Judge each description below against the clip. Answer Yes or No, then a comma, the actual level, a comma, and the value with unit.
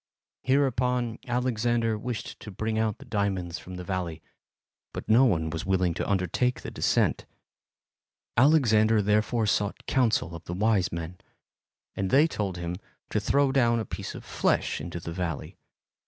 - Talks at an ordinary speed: Yes, average, 155 wpm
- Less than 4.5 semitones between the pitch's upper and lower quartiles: No, average, 4.8 semitones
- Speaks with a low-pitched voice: Yes, low, 105 Hz